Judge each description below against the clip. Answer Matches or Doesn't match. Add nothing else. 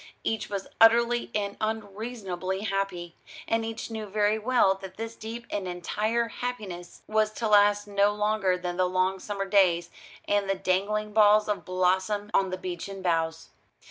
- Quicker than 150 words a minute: Matches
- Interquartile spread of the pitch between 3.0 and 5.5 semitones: Doesn't match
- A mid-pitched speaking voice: Doesn't match